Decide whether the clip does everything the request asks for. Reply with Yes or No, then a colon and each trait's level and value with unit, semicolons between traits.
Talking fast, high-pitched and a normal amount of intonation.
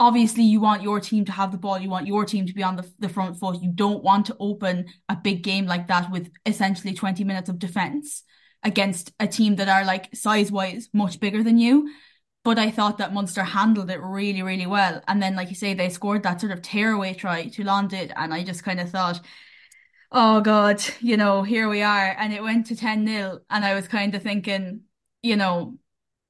No: fast, 225 wpm; high, 200 Hz; narrow, 2.2 semitones